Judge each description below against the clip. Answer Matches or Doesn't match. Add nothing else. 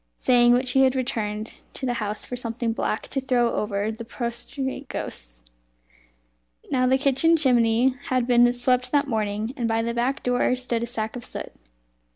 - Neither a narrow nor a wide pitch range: Doesn't match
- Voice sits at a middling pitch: Doesn't match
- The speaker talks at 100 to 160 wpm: Doesn't match